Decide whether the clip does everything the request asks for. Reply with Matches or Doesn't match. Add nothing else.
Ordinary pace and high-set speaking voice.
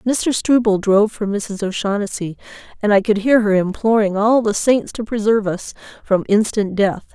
Matches